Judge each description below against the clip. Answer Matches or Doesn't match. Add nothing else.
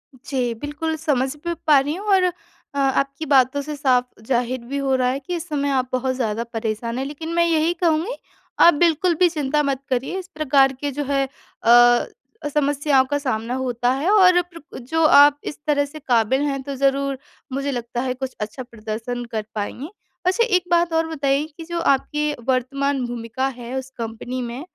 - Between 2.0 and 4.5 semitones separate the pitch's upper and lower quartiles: Matches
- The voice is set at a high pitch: Matches